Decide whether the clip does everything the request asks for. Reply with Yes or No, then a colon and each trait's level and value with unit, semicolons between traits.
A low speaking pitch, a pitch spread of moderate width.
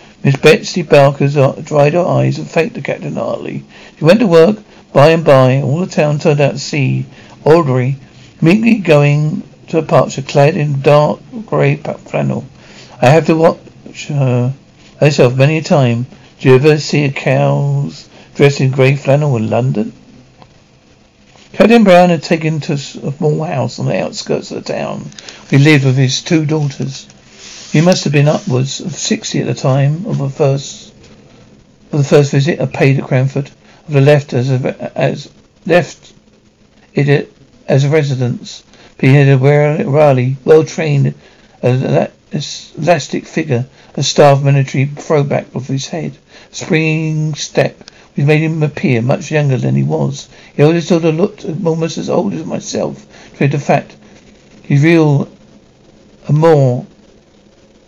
No: medium, 145 Hz; average, 3.0 semitones